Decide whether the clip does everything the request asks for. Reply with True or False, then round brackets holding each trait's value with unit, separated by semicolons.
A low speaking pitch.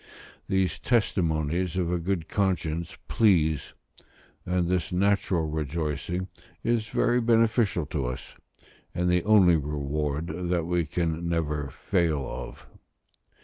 True (85 Hz)